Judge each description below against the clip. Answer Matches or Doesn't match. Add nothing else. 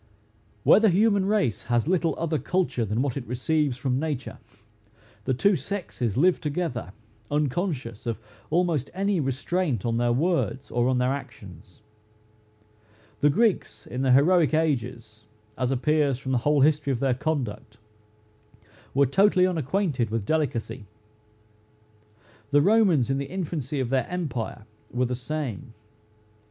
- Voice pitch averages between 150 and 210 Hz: Doesn't match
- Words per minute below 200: Matches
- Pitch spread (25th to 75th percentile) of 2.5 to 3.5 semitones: Doesn't match